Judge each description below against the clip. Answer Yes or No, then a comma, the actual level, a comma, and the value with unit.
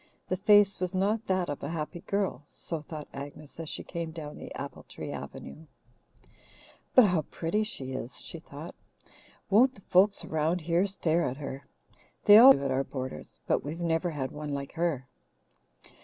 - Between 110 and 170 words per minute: No, average, 180 wpm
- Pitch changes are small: No, average, 4.4 semitones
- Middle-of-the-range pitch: Yes, medium, 165 Hz